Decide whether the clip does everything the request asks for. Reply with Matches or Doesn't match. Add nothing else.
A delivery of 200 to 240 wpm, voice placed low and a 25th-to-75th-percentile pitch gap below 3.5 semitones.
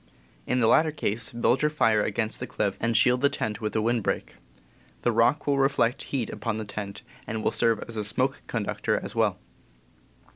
Matches